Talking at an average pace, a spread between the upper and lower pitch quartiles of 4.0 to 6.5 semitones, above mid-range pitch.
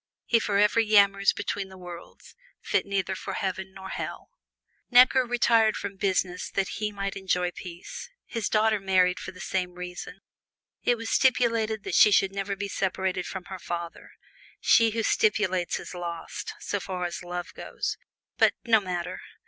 No: average, 165 wpm; average, 2.8 semitones; high, 195 Hz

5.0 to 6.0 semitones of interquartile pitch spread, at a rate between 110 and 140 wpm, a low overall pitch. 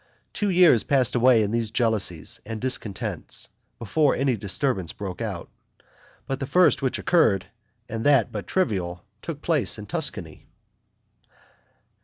Yes: wide, 5.6 semitones; slow, 135 wpm; low, 115 Hz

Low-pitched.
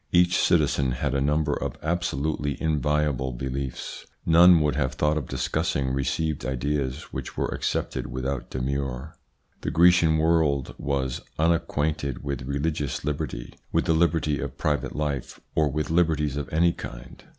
Yes: very low, 75 Hz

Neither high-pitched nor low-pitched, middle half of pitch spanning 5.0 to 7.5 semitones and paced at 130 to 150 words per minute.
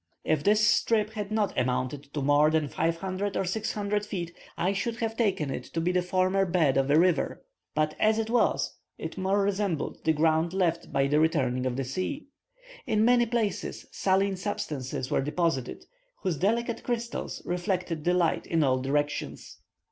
No: medium, 180 Hz; wide, 5.5 semitones; average, 175 wpm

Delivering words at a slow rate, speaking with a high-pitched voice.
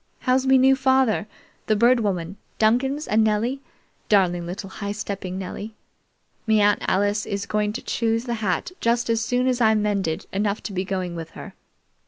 No: average, 180 wpm; high, 215 Hz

